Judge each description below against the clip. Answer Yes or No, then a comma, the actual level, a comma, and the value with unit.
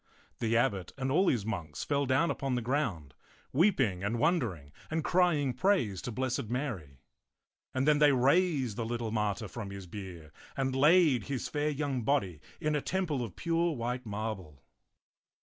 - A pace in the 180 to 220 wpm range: No, average, 165 wpm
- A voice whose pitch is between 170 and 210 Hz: No, low, 125 Hz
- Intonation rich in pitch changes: Yes, wide, 6.1 semitones